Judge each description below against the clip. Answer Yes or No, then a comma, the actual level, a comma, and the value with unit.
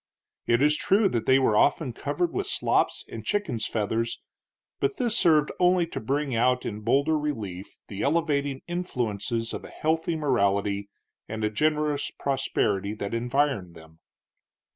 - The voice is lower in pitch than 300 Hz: Yes, low, 135 Hz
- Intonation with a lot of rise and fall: Yes, wide, 6.1 semitones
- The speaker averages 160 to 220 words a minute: No, average, 150 wpm